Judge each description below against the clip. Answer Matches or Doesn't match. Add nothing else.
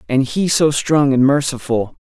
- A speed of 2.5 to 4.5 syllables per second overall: Matches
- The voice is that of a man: Matches